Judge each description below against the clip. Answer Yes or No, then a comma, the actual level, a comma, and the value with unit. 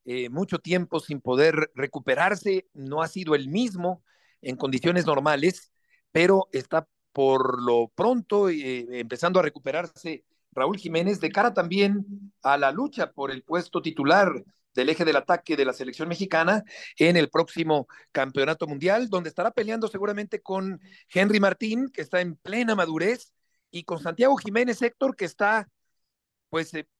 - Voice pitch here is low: No, medium, 170 Hz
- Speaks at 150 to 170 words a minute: Yes, average, 155 wpm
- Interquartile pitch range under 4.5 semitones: No, wide, 5.5 semitones